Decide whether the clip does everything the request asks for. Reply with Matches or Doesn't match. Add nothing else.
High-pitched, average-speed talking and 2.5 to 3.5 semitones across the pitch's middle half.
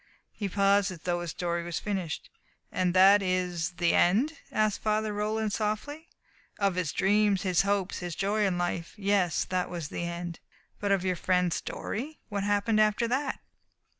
Matches